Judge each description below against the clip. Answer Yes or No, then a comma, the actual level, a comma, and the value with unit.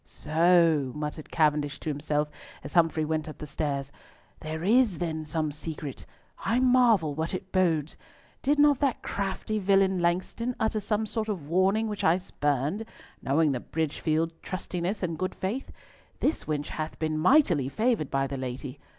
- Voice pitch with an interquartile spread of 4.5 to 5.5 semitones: Yes, average, 4.9 semitones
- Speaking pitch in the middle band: Yes, medium, 165 Hz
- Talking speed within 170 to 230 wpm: No, average, 160 wpm